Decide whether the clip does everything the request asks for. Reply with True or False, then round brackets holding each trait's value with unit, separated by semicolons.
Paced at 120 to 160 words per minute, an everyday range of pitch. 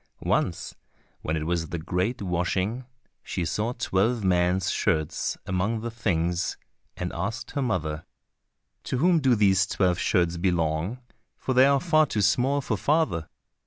False (150 wpm; 5.8 semitones)